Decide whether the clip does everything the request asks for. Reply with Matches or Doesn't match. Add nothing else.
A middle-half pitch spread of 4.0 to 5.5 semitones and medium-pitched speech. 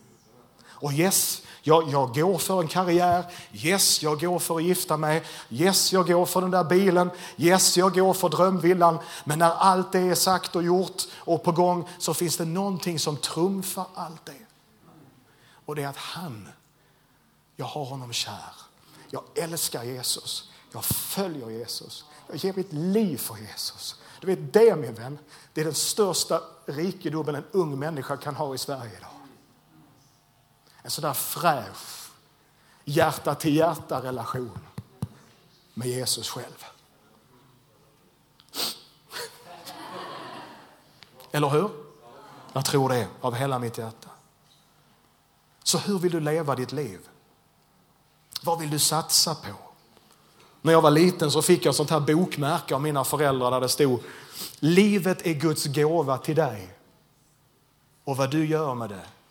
Matches